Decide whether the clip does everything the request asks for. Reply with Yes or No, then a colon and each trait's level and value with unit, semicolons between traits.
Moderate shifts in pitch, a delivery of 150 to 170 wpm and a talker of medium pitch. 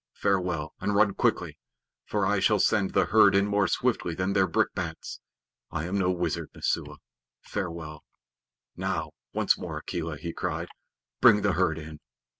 No: average, 3.3 semitones; average, 155 wpm; very low, 90 Hz